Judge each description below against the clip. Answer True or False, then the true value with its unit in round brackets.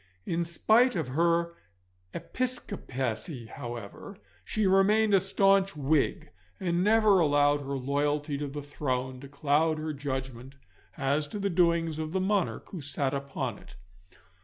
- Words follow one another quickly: False (140 wpm)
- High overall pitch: False (155 Hz)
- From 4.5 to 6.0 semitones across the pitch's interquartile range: True (5.4 semitones)